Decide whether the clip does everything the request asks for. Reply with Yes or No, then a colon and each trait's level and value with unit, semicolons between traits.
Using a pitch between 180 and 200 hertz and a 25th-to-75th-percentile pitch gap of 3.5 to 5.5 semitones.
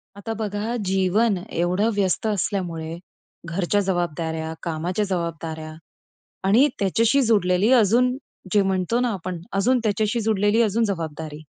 Yes: high, 195 Hz; average, 4.2 semitones